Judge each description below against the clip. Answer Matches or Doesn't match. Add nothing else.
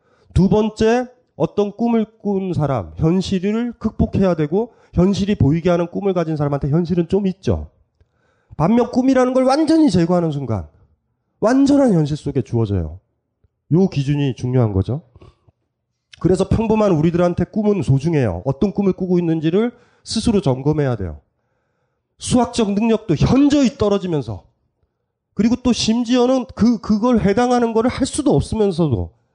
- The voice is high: Doesn't match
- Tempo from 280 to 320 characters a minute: Matches